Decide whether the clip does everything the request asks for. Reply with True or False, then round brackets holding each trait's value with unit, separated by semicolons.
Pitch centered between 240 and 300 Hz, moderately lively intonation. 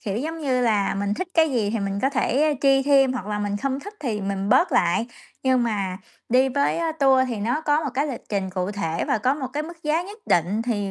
False (250 Hz; 6.0 semitones)